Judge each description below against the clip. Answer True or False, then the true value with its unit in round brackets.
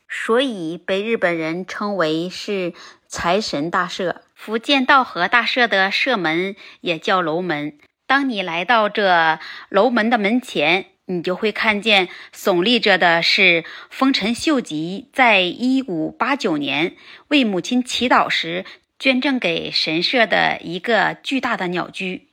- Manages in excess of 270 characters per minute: False (190 characters per minute)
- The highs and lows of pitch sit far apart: True (6.0 semitones)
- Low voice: False (200 Hz)